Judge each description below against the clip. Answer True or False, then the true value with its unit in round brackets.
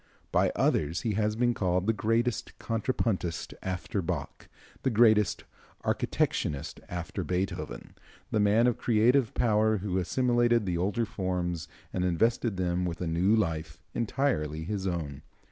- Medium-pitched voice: False (95 Hz)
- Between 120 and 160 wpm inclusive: True (140 wpm)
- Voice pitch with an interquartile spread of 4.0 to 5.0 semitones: True (4.5 semitones)